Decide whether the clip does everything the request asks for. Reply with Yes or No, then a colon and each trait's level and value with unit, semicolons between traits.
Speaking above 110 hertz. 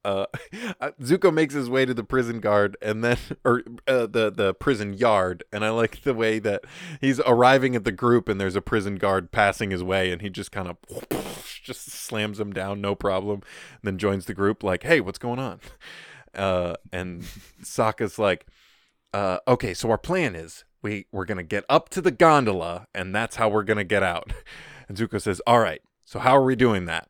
No: low, 105 Hz